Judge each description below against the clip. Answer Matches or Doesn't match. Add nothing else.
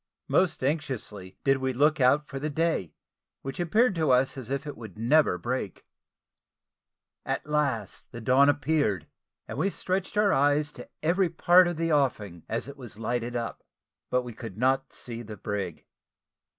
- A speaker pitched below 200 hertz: Matches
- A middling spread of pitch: Matches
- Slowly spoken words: Doesn't match